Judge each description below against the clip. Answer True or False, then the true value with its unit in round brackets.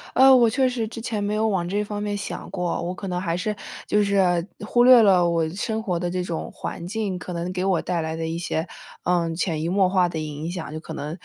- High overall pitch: False (180 Hz)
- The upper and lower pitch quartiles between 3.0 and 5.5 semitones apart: True (3.6 semitones)